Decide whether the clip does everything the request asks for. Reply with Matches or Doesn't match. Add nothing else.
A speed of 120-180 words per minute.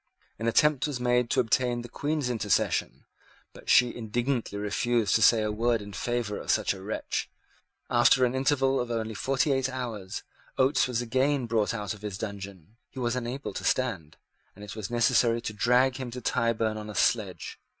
Doesn't match